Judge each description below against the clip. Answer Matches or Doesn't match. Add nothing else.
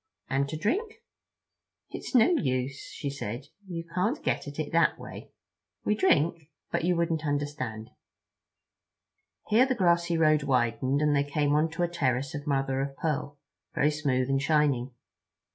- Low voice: Doesn't match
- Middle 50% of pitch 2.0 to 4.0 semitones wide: Matches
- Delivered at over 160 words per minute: Doesn't match